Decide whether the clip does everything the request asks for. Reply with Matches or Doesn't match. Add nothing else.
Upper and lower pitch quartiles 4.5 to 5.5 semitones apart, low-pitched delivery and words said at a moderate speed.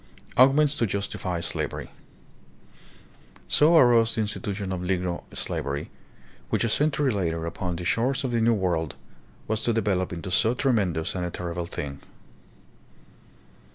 Matches